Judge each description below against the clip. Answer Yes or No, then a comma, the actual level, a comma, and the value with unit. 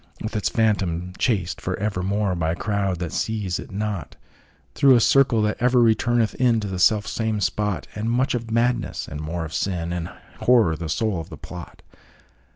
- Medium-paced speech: Yes, average, 165 wpm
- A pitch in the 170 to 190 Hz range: No, low, 105 Hz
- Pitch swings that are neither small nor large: Yes, average, 4.3 semitones